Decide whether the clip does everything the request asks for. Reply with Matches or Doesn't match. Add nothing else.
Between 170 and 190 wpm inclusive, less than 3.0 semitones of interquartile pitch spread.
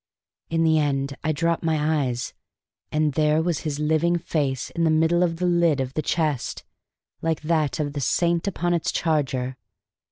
Matches